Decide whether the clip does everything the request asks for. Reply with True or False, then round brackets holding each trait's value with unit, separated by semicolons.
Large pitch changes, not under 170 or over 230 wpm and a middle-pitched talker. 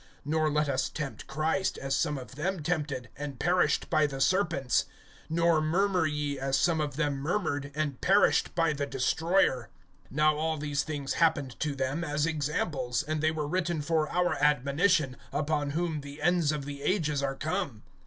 False (2.7 semitones; 175 wpm; 150 Hz)